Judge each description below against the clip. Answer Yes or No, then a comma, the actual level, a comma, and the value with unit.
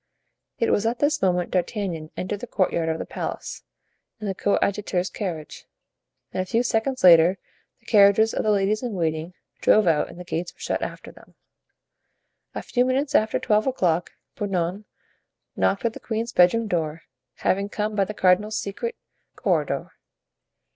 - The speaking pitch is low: No, high, 200 Hz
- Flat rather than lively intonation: No, average, 3.7 semitones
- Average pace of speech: Yes, average, 165 wpm